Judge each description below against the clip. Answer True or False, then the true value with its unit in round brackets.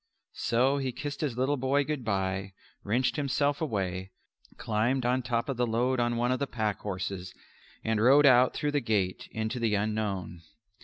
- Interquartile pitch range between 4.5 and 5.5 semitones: False (4.0 semitones)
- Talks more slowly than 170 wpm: False (175 wpm)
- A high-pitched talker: False (120 Hz)